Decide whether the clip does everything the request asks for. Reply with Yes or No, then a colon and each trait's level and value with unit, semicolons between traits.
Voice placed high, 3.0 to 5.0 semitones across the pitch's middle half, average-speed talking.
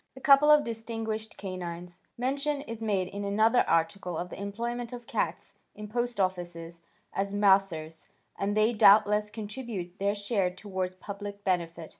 Yes: high, 205 Hz; average, 3.5 semitones; average, 150 wpm